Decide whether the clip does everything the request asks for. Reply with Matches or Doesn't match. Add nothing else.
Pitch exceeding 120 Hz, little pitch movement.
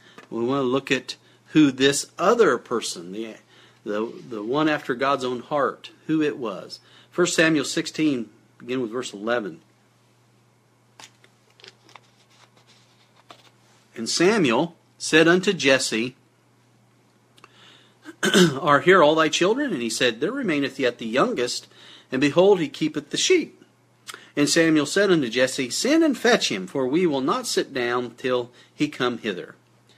Doesn't match